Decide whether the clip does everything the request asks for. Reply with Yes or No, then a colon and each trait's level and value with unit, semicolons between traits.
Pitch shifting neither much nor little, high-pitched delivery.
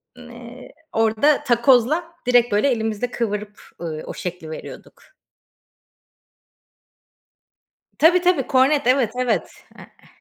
Yes: average, 3.6 semitones; high, 240 Hz